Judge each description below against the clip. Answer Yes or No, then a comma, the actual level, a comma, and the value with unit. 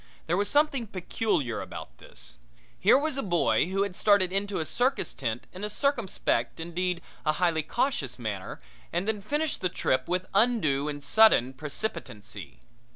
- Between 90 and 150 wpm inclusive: No, average, 160 wpm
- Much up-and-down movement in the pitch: Yes, wide, 7.5 semitones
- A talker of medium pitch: Yes, medium, 180 Hz